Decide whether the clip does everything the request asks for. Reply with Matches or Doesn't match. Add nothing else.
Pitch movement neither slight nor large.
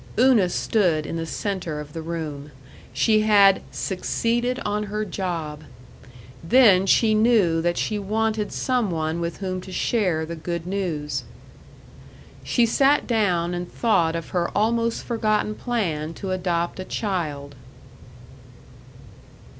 Matches